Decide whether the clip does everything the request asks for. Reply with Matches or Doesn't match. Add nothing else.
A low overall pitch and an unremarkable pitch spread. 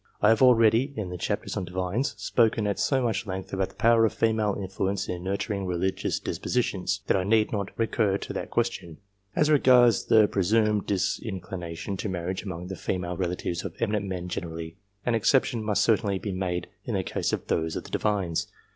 Matches